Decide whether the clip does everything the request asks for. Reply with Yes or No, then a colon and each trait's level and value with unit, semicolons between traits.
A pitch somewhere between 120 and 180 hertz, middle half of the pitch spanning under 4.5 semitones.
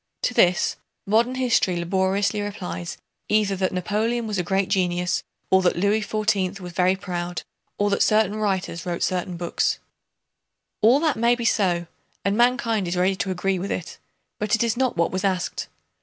No: high, 195 Hz; average, 3.2 semitones